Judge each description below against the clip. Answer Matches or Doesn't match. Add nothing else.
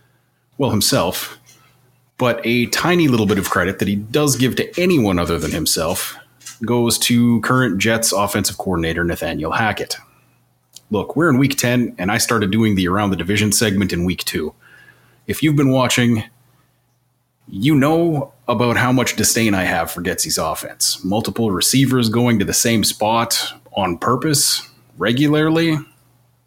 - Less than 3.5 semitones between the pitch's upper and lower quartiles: Doesn't match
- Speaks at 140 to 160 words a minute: Matches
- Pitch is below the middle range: Matches